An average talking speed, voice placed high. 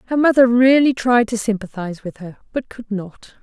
Yes: average, 195 wpm; high, 225 Hz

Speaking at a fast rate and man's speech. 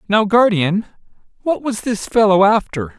No: average, 140 wpm; male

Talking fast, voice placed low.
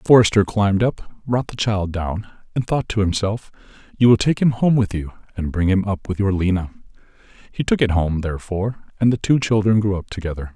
Yes: fast, 215 wpm; low, 105 Hz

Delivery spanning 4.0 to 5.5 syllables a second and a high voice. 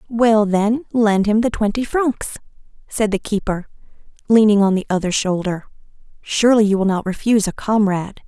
Yes: 5.2 syllables/s; high, 210 Hz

